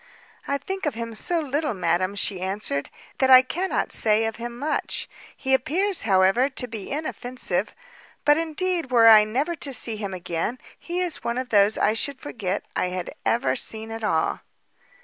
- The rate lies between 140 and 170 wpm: No, average, 180 wpm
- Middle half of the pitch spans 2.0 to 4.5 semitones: No, wide, 5.6 semitones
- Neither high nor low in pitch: No, high, 235 Hz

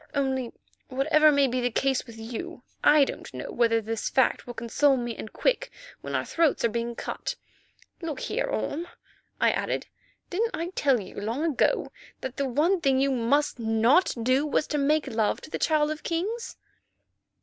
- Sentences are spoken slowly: No, average, 180 wpm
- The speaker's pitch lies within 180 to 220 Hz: No, very high, 275 Hz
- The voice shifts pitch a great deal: No, average, 4.5 semitones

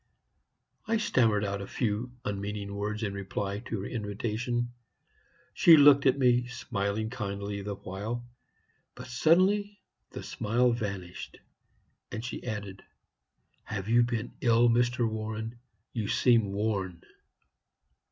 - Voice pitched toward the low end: Yes, low, 110 Hz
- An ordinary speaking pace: No, slow, 125 wpm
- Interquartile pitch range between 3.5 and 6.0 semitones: No, average, 3.1 semitones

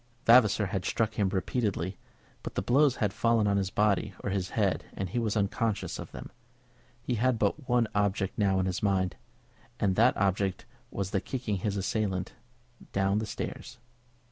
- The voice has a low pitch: Yes, low, 100 Hz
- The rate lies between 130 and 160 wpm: No, average, 175 wpm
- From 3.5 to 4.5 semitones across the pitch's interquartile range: No, average, 2.9 semitones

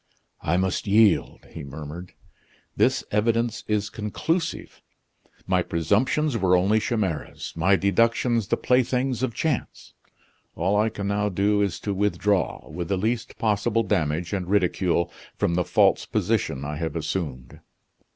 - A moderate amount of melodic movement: Yes, average, 4.4 semitones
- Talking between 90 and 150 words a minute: Yes, average, 140 wpm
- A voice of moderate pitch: No, low, 100 Hz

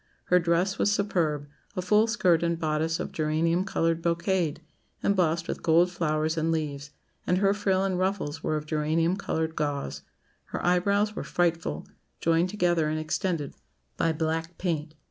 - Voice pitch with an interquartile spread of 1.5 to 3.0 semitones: Yes, average, 2.7 semitones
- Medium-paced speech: Yes, average, 160 wpm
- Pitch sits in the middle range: Yes, medium, 165 Hz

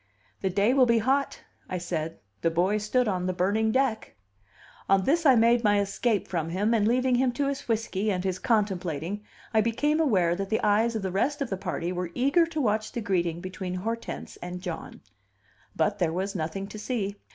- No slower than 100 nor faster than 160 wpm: No, fast, 205 wpm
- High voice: Yes, high, 205 Hz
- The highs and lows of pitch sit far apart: No, average, 4.4 semitones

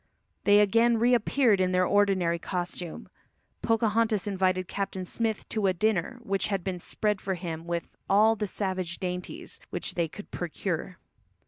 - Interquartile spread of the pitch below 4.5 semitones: Yes, average, 2.9 semitones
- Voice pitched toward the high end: Yes, high, 195 Hz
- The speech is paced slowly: No, average, 150 wpm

